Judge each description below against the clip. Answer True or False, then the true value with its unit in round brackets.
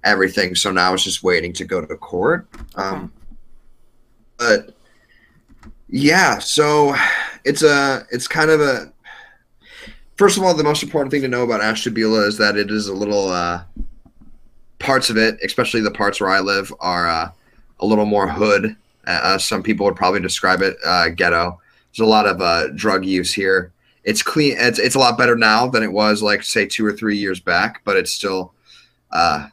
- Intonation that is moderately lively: True (4.4 semitones)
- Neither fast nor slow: True (185 wpm)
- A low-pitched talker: True (110 Hz)